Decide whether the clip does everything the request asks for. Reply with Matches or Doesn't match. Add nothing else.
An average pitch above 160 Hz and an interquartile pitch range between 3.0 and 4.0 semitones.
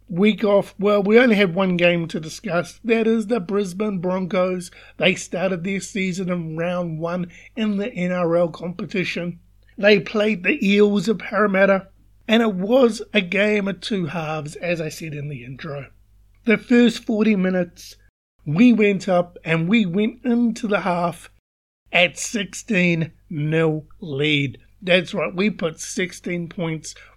Matches